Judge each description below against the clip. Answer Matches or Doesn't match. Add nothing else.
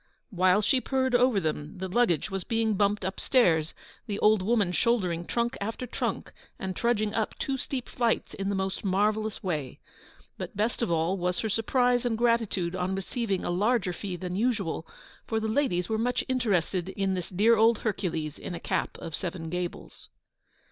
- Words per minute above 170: Matches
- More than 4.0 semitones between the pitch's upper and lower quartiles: Matches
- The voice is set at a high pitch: Matches